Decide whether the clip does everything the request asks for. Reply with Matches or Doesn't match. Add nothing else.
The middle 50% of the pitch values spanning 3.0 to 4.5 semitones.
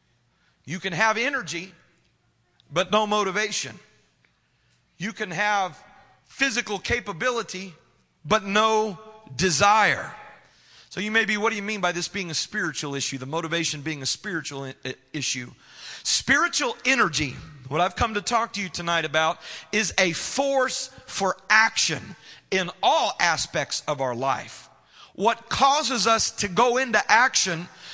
Doesn't match